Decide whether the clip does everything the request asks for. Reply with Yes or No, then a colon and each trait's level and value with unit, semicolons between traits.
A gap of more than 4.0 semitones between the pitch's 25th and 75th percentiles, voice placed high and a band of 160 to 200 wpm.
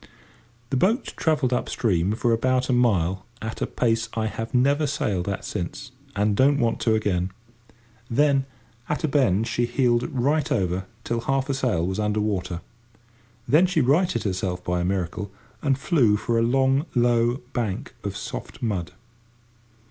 No: average, 5.2 semitones; low, 115 Hz; average, 165 wpm